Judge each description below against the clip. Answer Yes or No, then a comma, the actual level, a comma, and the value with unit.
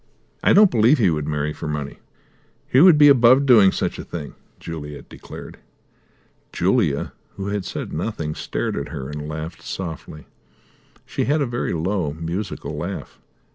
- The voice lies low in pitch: Yes, very low, 85 Hz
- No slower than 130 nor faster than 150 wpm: No, average, 160 wpm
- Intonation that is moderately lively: No, wide, 7.4 semitones